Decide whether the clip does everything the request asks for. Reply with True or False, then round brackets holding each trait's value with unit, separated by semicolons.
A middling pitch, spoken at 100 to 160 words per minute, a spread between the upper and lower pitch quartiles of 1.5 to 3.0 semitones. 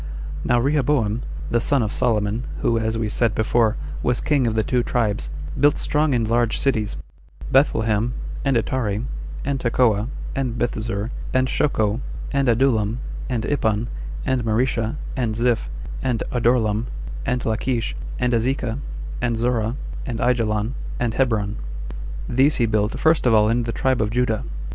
False (120 Hz; 150 wpm; 2.6 semitones)